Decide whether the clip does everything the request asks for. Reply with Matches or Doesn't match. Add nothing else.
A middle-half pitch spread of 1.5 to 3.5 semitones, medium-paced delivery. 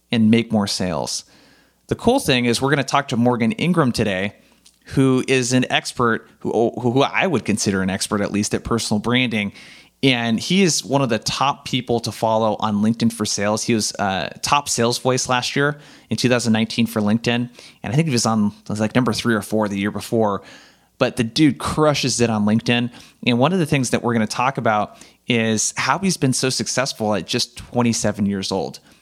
Doesn't match